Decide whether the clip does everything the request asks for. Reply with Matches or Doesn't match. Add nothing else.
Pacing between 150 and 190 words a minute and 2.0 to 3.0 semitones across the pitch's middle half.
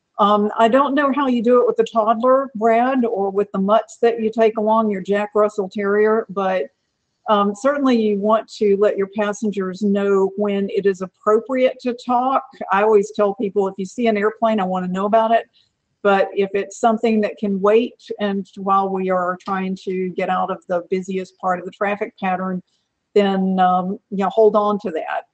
Doesn't match